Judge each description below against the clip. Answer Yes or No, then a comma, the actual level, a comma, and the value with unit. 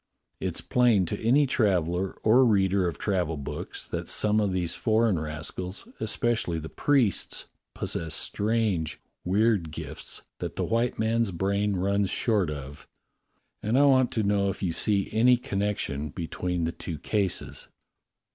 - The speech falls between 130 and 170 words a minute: Yes, average, 150 wpm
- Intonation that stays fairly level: No, average, 4.1 semitones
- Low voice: Yes, low, 100 Hz